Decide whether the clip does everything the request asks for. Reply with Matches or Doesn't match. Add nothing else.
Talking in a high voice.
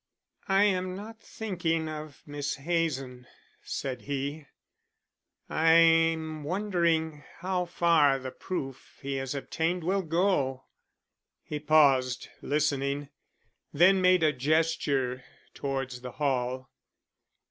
Doesn't match